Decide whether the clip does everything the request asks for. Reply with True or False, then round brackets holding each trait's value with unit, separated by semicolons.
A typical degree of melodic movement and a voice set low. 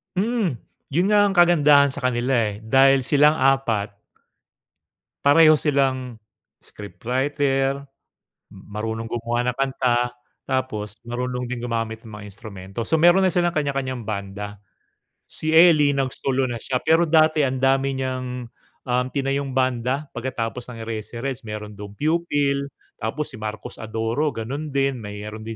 True (4.0 semitones; 130 Hz)